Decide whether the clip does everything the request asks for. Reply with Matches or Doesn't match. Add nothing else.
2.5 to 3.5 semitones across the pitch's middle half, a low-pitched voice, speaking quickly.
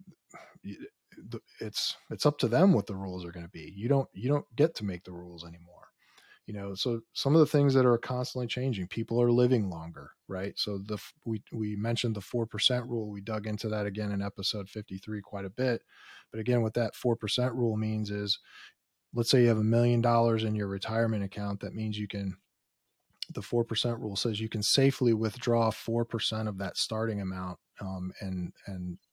Matches